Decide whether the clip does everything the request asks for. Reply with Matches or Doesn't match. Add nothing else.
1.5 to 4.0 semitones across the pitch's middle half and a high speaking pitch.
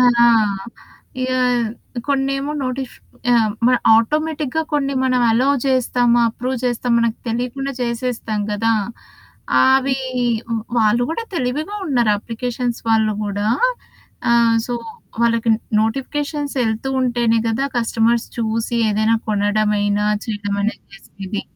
Matches